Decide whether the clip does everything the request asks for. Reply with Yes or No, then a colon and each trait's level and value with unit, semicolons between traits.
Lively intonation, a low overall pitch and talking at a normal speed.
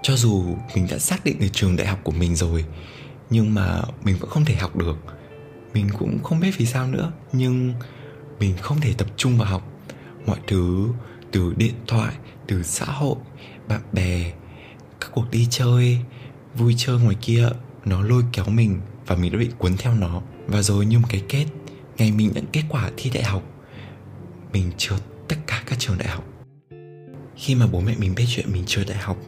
No: average, 5.0 semitones; low, 115 Hz; average, 200 wpm